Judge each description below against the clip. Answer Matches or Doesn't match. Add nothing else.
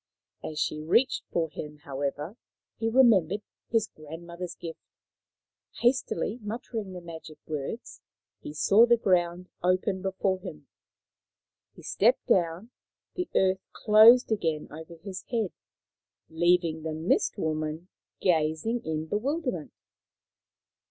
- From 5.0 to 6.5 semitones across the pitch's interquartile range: Matches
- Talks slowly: Matches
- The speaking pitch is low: Doesn't match